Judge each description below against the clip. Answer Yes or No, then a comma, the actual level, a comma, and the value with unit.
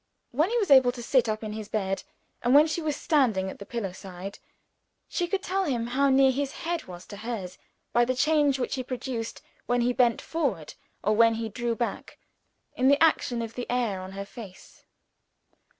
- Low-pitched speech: No, high, 240 Hz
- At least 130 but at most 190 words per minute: No, fast, 205 wpm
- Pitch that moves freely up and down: No, average, 4.5 semitones